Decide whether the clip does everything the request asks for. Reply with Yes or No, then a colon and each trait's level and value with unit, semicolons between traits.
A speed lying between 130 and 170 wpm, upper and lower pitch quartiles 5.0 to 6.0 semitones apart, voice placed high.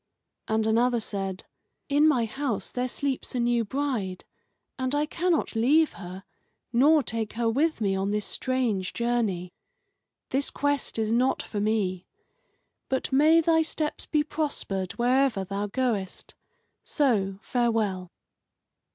Yes: slow, 135 wpm; wide, 5.6 semitones; high, 235 Hz